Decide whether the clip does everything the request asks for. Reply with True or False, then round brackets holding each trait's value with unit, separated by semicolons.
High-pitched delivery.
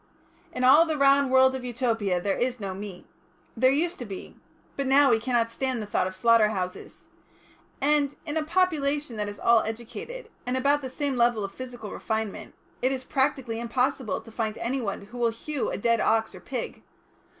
True (245 Hz)